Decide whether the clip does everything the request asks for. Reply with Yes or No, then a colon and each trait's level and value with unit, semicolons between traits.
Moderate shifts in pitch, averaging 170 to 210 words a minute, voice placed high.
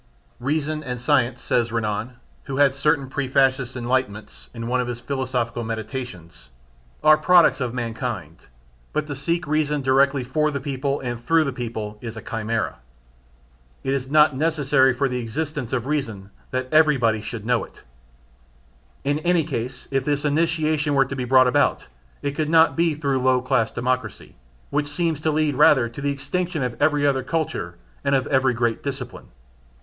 No: average, 3.5 semitones; average, 175 wpm; low, 135 Hz